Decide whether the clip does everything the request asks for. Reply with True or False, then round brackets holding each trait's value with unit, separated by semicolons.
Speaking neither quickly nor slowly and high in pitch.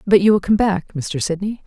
False (250 wpm; 195 Hz)